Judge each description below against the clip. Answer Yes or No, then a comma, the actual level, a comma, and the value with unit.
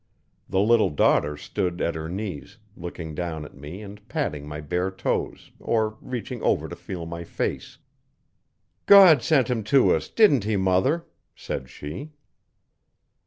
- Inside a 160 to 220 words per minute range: No, average, 150 wpm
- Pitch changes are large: Yes, wide, 6.5 semitones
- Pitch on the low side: Yes, very low, 95 Hz